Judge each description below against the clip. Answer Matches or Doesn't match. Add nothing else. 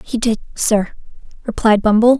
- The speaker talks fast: Doesn't match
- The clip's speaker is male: Doesn't match